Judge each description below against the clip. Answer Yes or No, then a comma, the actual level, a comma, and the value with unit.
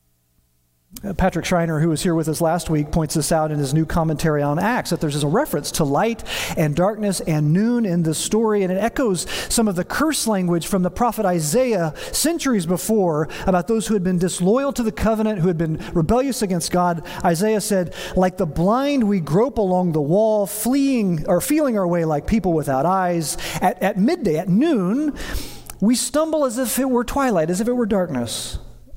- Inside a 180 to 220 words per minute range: Yes, average, 200 wpm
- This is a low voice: No, medium, 185 Hz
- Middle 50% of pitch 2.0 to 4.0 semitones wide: No, average, 5.1 semitones